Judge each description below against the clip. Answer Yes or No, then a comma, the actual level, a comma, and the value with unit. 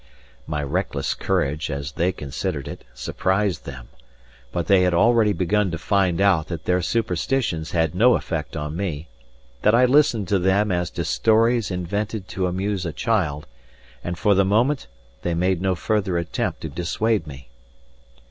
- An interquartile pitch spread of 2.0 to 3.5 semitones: No, average, 4.2 semitones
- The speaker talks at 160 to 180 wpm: Yes, average, 165 wpm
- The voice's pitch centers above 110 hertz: No, very low, 90 Hz